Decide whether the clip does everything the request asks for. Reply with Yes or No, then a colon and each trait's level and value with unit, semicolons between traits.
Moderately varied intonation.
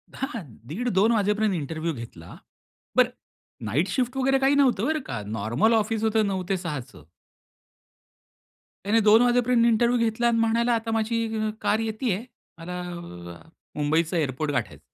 No: wide, 6.2 semitones